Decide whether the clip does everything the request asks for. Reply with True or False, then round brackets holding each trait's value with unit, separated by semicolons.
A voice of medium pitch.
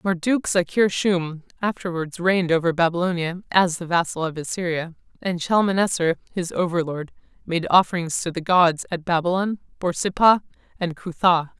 True (175 Hz)